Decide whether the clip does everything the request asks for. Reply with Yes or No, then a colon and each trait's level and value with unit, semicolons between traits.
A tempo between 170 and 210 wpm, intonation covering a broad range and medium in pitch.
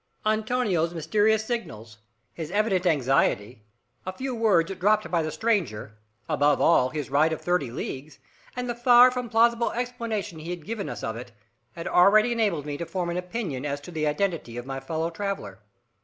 Yes: average, 180 wpm; wide, 6.8 semitones; medium, 175 Hz